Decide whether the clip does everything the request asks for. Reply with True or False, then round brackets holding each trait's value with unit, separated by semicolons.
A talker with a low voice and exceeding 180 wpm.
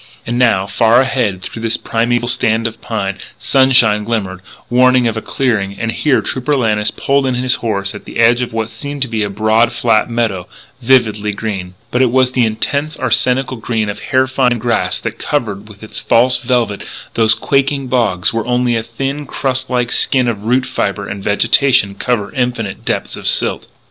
True (115 Hz; 190 wpm)